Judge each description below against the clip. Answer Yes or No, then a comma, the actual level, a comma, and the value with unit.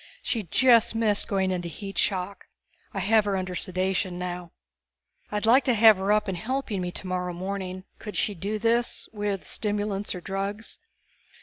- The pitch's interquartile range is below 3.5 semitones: Yes, narrow, 2.6 semitones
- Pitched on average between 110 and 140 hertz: No, high, 200 Hz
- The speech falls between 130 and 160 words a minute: No, average, 170 wpm